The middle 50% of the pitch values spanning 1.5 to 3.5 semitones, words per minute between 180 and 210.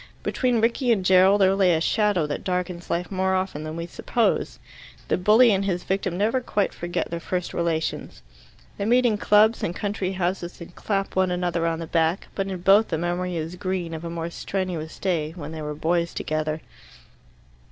Yes: average, 2.7 semitones; average, 195 wpm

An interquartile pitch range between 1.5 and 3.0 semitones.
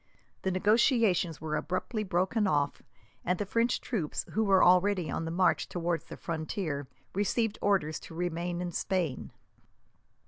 No: average, 3.7 semitones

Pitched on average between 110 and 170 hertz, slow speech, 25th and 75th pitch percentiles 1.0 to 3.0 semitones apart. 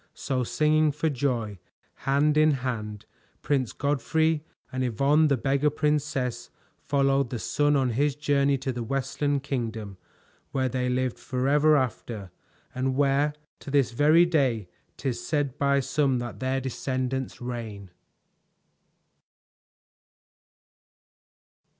Yes: low, 135 Hz; slow, 120 wpm; narrow, 2.6 semitones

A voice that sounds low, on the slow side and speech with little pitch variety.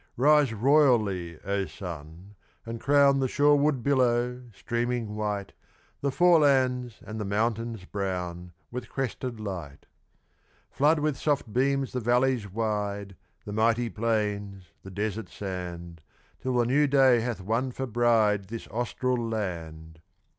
No: low, 115 Hz; slow, 130 wpm; average, 4.4 semitones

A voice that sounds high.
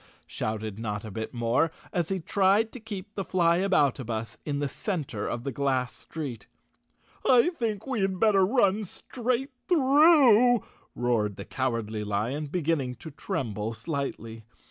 No: medium, 155 Hz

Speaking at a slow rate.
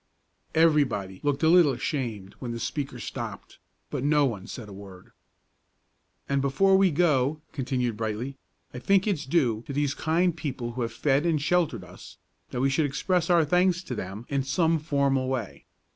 No: average, 175 wpm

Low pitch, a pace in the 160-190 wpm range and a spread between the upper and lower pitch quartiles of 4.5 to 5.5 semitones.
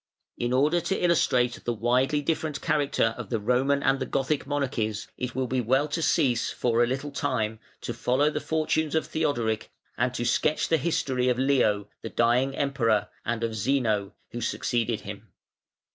No: low, 130 Hz; average, 175 wpm; average, 3.5 semitones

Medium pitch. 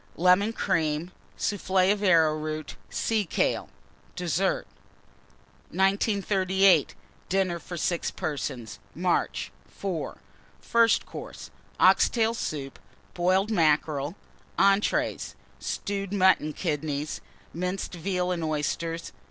Yes: medium, 180 Hz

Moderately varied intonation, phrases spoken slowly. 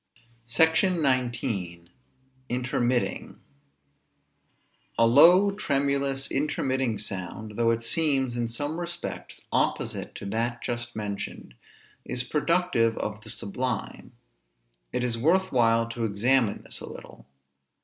Yes: average, 3.5 semitones; slow, 110 wpm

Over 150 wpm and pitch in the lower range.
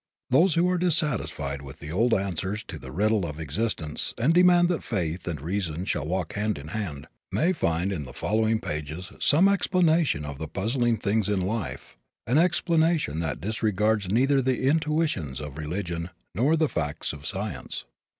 Yes: average, 170 wpm; low, 100 Hz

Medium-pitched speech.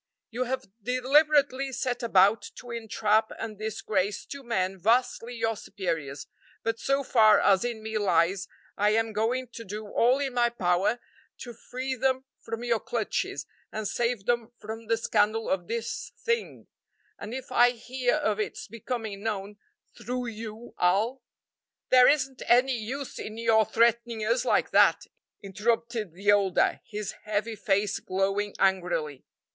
No: high, 225 Hz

